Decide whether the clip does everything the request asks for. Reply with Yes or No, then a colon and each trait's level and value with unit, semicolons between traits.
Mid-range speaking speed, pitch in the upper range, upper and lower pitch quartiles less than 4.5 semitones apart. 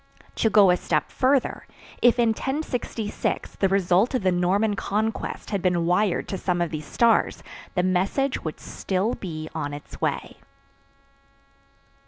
Yes: average, 150 wpm; high, 195 Hz; average, 4.0 semitones